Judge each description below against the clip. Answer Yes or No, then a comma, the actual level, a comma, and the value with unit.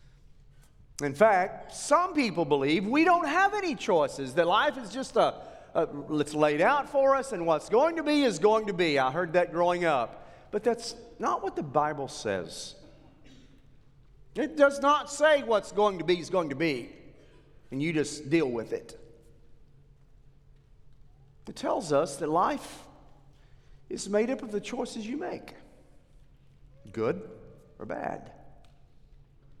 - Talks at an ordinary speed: Yes, average, 155 wpm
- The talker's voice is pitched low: No, medium, 160 Hz